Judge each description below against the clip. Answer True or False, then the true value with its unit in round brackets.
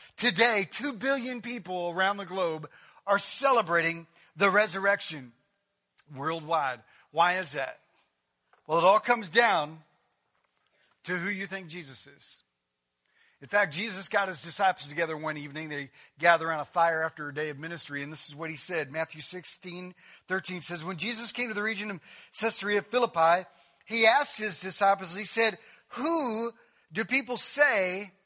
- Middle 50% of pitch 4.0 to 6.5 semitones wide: True (5.0 semitones)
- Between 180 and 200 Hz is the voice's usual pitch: True (185 Hz)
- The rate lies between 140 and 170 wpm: True (155 wpm)